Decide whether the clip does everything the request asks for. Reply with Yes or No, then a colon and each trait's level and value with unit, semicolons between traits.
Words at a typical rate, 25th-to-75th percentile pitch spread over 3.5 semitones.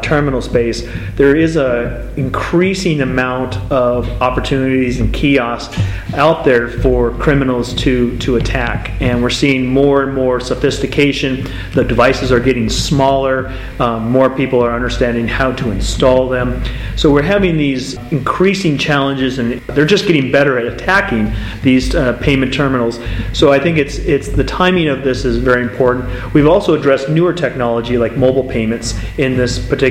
No: average, 160 wpm; narrow, 2.6 semitones